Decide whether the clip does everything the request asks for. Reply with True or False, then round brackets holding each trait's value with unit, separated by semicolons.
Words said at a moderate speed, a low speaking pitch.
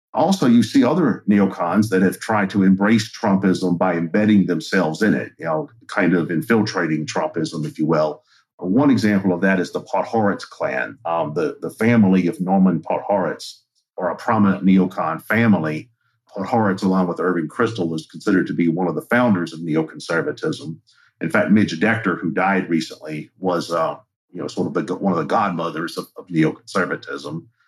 True (175 wpm; 95 Hz)